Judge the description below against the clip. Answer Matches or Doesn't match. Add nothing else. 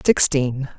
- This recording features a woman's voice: Matches